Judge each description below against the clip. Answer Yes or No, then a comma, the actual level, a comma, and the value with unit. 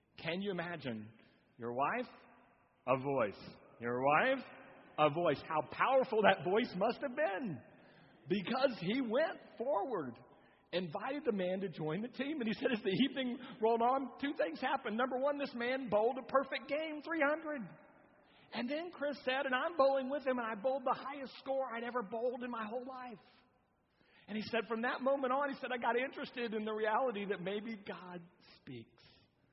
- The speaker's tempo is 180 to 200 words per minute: Yes, average, 185 wpm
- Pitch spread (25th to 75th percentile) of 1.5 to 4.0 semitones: No, average, 5.1 semitones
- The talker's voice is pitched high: Yes, high, 240 Hz